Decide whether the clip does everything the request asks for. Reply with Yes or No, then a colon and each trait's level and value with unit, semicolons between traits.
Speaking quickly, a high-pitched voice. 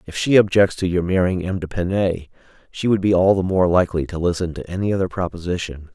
No: fast, 210 wpm; very low, 90 Hz